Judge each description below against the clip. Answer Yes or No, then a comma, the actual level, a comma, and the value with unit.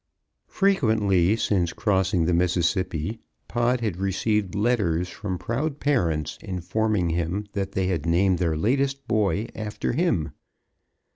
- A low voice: Yes, very low, 95 Hz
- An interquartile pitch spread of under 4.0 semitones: No, average, 4.3 semitones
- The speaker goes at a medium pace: No, slow, 130 wpm